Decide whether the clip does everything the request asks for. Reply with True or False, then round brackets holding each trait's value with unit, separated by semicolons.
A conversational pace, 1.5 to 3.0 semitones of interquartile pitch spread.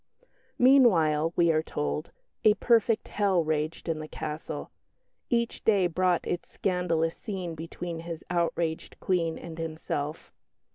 False (130 wpm; 2.7 semitones)